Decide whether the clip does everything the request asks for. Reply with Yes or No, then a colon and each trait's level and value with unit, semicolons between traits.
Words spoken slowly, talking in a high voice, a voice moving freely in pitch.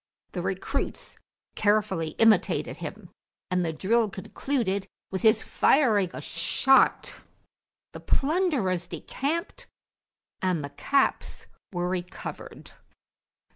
Yes: slow, 95 wpm; high, 205 Hz; wide, 6.5 semitones